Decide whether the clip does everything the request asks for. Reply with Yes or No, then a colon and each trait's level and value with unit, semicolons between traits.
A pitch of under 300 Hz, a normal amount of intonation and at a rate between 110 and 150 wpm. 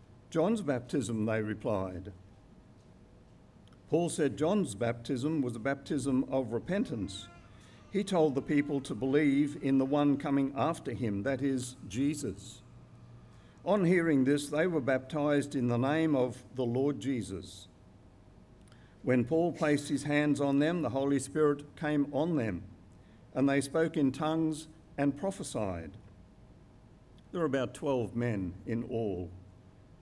Yes: low, 135 Hz; average, 4.9 semitones; slow, 135 wpm